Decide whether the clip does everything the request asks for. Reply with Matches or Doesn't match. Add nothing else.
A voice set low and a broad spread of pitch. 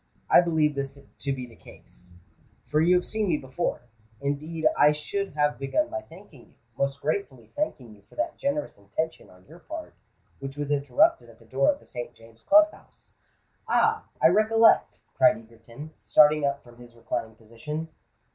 Doesn't match